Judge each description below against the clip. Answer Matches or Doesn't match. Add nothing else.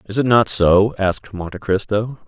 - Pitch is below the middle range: Matches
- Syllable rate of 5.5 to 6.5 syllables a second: Doesn't match